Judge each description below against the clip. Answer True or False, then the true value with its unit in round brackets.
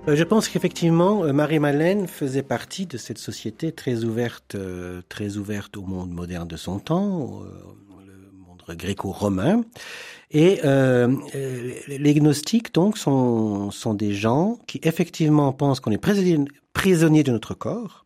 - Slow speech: True (135 wpm)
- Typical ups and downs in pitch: False (8.3 semitones)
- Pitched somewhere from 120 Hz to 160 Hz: True (135 Hz)